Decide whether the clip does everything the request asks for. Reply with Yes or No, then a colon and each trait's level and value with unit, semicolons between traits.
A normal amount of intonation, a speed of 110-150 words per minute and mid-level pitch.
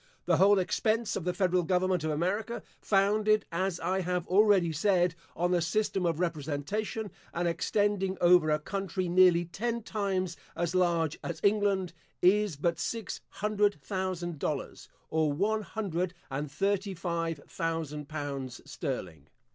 Yes: average, 3.4 semitones; average, 145 wpm; medium, 180 Hz